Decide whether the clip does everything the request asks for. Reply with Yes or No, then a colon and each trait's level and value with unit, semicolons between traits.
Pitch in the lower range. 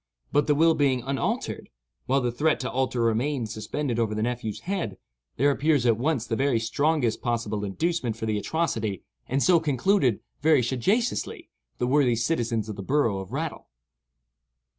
Yes: low, 125 Hz